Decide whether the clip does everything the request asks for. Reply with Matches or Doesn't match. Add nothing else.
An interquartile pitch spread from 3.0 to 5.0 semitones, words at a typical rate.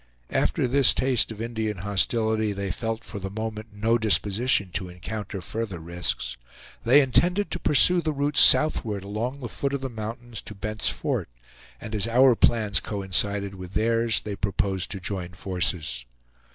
Matches